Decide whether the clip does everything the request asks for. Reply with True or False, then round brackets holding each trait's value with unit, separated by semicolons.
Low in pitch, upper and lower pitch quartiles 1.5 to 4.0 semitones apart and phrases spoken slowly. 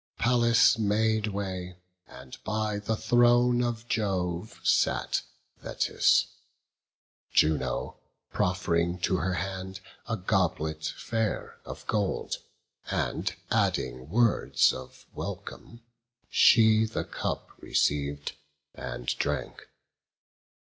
False (100 Hz; 4.8 semitones; 95 wpm)